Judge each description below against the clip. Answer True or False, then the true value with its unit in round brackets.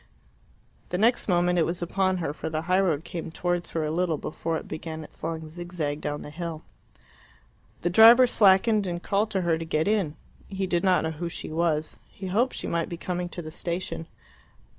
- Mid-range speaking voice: True (175 Hz)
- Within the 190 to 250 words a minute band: True (205 wpm)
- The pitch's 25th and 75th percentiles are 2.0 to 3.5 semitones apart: True (2.7 semitones)